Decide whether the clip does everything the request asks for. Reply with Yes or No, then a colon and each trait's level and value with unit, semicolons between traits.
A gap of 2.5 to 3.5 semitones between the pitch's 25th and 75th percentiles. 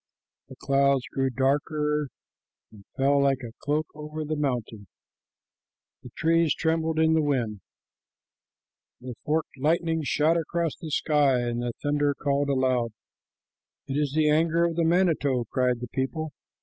Yes: average, 3.2 semitones